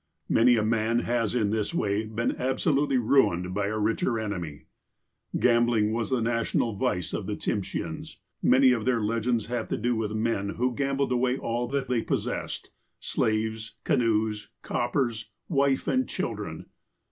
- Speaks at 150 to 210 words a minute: Yes, average, 160 wpm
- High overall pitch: No, low, 115 Hz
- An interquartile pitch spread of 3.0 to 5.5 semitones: No, narrow, 2.5 semitones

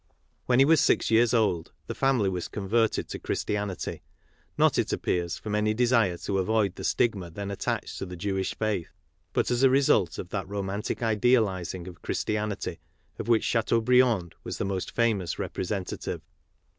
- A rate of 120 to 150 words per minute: No, average, 170 wpm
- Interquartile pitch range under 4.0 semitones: Yes, average, 3.5 semitones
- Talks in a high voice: No, low, 105 Hz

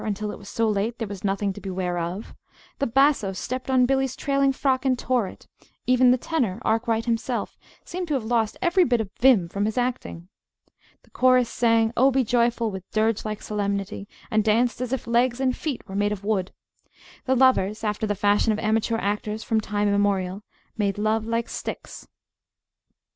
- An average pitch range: Yes, average, 3.6 semitones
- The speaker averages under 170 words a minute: No, average, 190 wpm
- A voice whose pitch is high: Yes, high, 225 Hz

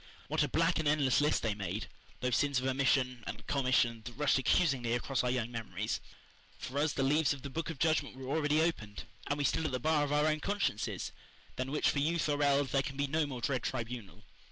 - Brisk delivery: Yes, fast, 230 wpm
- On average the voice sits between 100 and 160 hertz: Yes, medium, 140 Hz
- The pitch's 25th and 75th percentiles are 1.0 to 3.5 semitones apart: Yes, average, 2.9 semitones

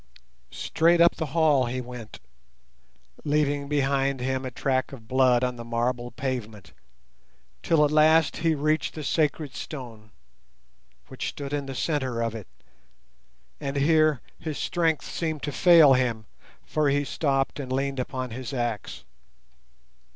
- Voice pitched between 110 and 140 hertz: Yes, low, 135 Hz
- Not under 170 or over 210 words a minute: No, average, 145 wpm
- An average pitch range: Yes, average, 3.4 semitones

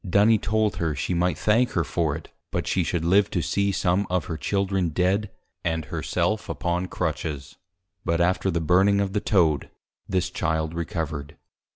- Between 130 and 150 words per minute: No, average, 180 wpm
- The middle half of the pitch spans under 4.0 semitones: Yes, average, 3.4 semitones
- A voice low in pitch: Yes, very low, 90 Hz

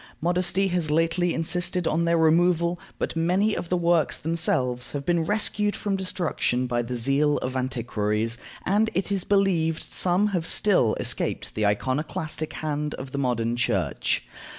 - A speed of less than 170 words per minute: Yes, average, 155 wpm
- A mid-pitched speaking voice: Yes, medium, 165 Hz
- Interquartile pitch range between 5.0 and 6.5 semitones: Yes, wide, 5.6 semitones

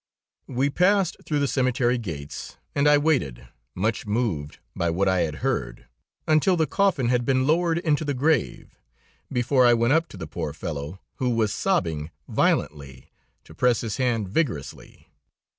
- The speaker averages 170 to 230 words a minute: No, average, 160 wpm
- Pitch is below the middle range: Yes, low, 120 Hz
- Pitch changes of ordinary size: No, wide, 8.2 semitones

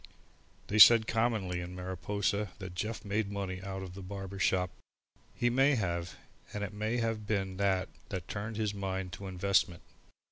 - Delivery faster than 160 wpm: Yes, average, 170 wpm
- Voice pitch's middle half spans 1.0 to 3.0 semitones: Yes, narrow, 2.5 semitones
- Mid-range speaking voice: No, low, 100 Hz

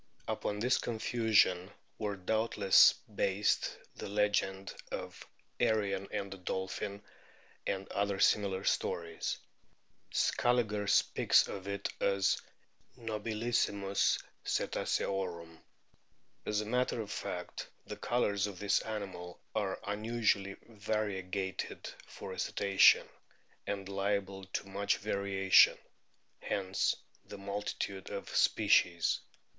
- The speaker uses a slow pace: Yes, slow, 105 wpm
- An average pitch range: No, narrow, 1.6 semitones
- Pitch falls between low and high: No, low, 100 Hz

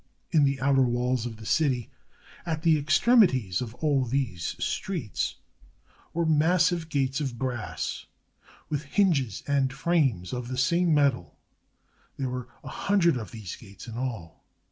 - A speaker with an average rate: Yes, average, 145 wpm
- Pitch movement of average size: Yes, average, 4.7 semitones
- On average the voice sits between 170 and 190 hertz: No, low, 135 Hz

